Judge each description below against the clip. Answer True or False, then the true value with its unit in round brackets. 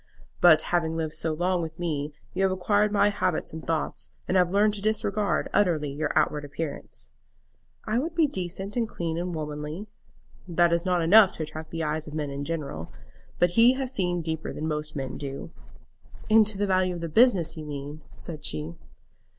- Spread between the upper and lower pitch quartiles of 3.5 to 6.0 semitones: True (4.2 semitones)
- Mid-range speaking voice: True (170 Hz)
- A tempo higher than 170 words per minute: True (190 wpm)